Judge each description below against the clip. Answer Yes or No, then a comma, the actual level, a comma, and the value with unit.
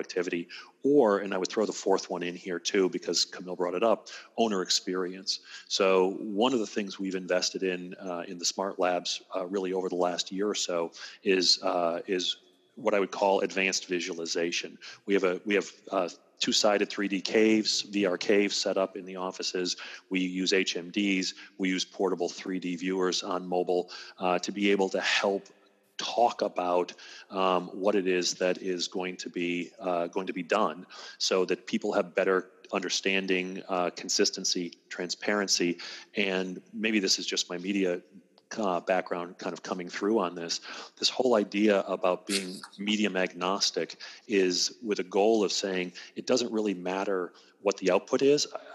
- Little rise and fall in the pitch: Yes, narrow, 1.7 semitones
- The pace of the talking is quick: No, average, 180 wpm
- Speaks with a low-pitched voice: Yes, very low, 95 Hz